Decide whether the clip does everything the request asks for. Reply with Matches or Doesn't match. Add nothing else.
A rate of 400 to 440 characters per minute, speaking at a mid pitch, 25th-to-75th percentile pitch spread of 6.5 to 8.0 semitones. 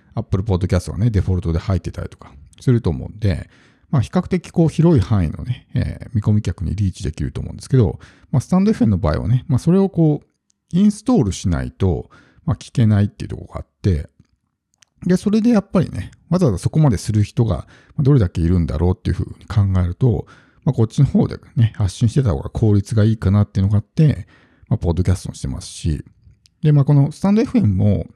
Doesn't match